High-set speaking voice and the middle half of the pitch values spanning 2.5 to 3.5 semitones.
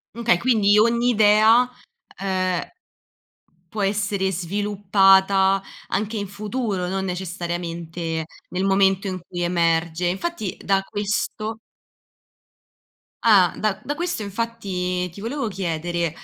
Yes: high, 195 Hz; average, 2.9 semitones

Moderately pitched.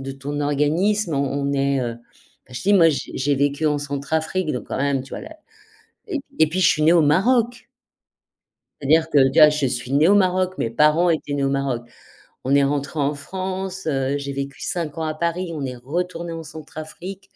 Yes: medium, 150 Hz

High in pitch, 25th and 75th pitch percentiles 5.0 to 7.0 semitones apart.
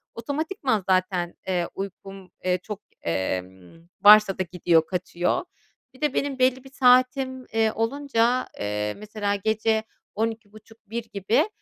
Yes: high, 215 Hz; average, 5.3 semitones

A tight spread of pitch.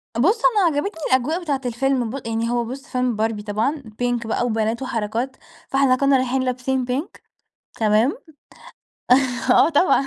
No: average, 3.2 semitones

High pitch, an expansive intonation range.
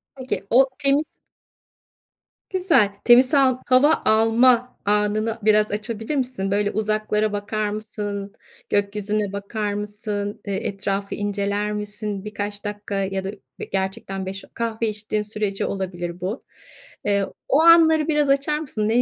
No: high, 210 Hz; average, 2.8 semitones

